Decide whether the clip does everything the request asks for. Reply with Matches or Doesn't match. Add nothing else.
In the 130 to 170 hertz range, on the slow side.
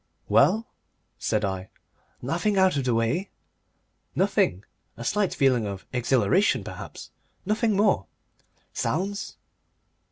Matches